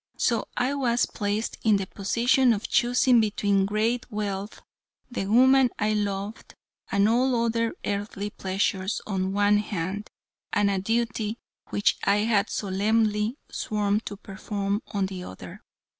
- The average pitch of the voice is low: No, high, 210 Hz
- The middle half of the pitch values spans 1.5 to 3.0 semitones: Yes, narrow, 2.5 semitones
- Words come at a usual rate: Yes, average, 145 wpm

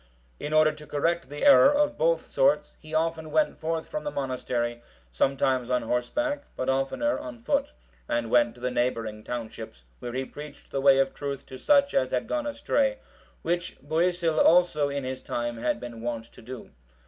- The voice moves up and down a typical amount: No, wide, 5.9 semitones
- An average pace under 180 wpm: No, average, 185 wpm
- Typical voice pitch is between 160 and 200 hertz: No, medium, 140 Hz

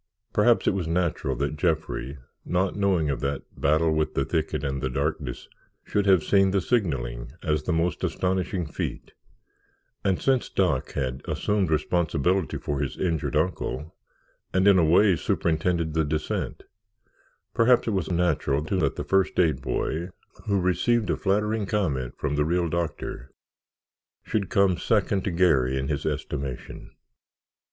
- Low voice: Yes, very low, 85 Hz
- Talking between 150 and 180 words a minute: Yes, average, 155 wpm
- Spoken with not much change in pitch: No, average, 4.4 semitones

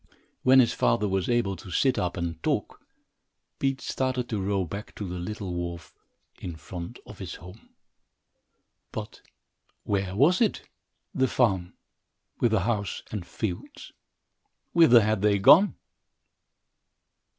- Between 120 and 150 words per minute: Yes, slow, 135 wpm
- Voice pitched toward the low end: Yes, low, 100 Hz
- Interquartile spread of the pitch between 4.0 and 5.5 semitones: Yes, average, 4.9 semitones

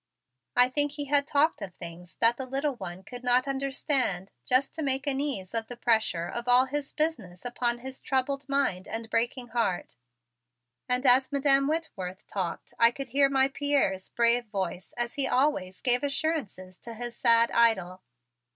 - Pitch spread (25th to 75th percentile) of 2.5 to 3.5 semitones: No, average, 4.0 semitones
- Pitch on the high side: Yes, high, 245 Hz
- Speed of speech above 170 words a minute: Yes, average, 180 wpm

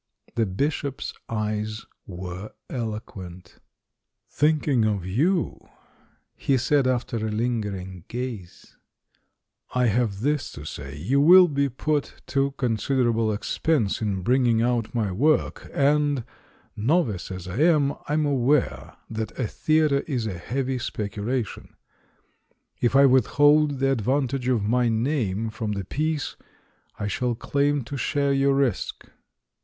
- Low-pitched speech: Yes, low, 125 Hz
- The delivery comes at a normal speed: No, slow, 130 wpm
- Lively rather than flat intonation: No, average, 4.8 semitones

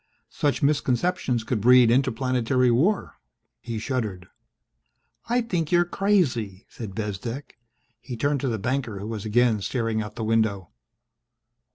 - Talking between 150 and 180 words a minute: No, slow, 135 wpm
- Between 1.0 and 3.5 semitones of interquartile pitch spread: No, average, 4.1 semitones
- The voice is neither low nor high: No, low, 120 Hz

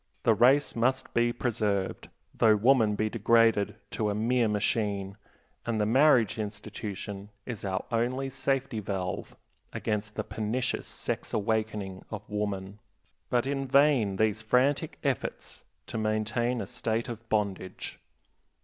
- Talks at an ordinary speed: No, slow, 130 wpm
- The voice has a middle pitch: No, low, 110 Hz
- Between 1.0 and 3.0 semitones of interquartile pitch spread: Yes, average, 2.7 semitones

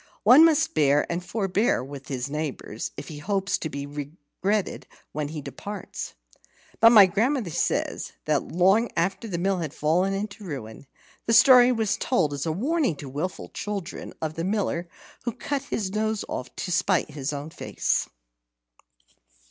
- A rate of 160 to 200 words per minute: Yes, average, 165 wpm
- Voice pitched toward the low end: No, medium, 180 Hz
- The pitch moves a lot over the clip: Yes, wide, 6.3 semitones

